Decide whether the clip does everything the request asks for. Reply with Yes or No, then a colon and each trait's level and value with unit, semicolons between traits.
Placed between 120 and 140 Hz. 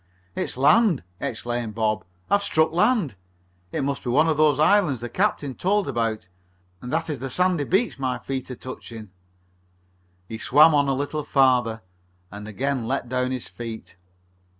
Yes: low, 135 Hz